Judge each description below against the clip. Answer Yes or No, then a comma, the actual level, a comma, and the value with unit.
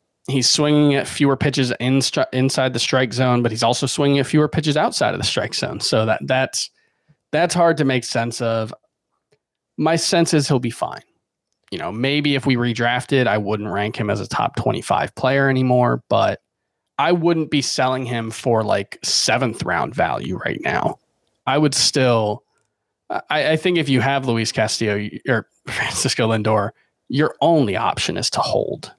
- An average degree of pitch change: Yes, average, 4.0 semitones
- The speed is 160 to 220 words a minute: Yes, average, 180 wpm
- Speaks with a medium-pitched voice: No, low, 130 Hz